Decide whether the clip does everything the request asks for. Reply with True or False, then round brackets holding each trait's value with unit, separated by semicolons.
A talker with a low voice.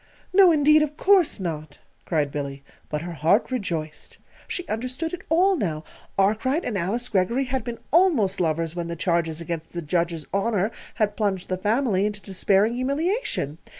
False (200 Hz)